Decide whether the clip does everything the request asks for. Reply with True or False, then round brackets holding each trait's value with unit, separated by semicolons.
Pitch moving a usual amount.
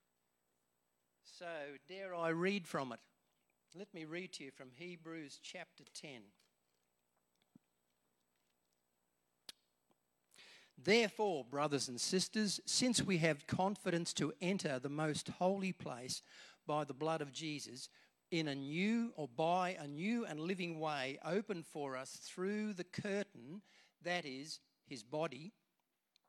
False (7.9 semitones)